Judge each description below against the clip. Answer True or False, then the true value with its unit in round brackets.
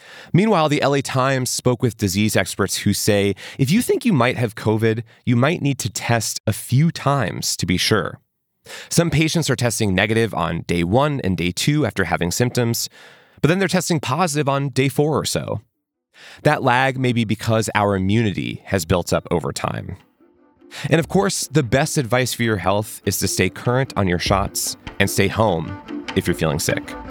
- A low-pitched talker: True (120 Hz)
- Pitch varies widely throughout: True (6.6 semitones)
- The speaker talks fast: False (195 wpm)